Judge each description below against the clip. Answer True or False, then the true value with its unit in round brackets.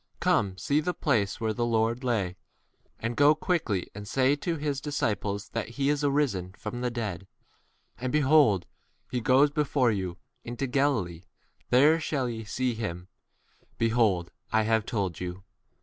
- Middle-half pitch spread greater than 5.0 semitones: True (5.4 semitones)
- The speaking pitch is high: False (120 Hz)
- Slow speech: False (150 wpm)